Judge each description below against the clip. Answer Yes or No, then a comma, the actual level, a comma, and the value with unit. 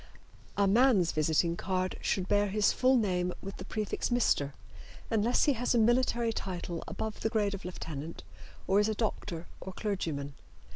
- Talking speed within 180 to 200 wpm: No, average, 165 wpm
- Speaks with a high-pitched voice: Yes, high, 200 Hz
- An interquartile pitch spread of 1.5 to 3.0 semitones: No, average, 3.8 semitones